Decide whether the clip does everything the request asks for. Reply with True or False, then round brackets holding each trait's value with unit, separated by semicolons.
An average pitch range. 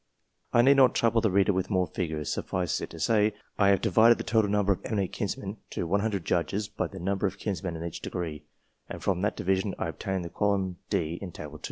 True (3.0 semitones)